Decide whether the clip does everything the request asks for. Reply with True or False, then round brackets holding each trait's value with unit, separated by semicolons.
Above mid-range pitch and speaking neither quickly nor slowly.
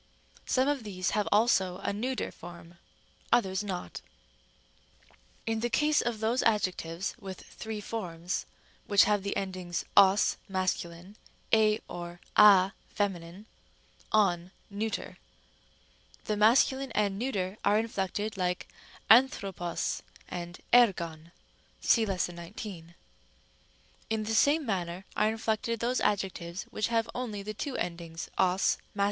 False (200 Hz; 125 wpm)